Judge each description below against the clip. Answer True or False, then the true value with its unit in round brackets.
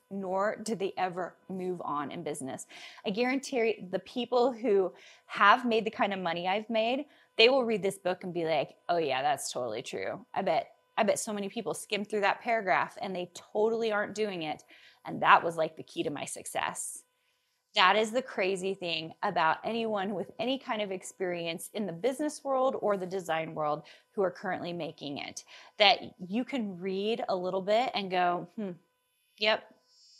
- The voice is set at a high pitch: True (205 Hz)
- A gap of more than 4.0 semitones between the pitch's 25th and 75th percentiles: True (4.4 semitones)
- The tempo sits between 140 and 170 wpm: False (190 wpm)